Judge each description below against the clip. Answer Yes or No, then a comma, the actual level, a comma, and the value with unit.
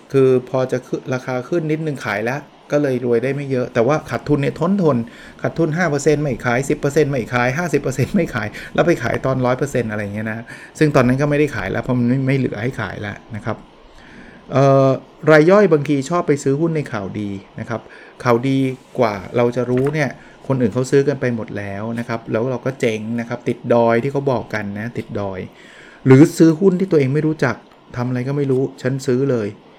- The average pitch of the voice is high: No, low, 130 Hz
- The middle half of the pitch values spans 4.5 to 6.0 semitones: No, average, 3.7 semitones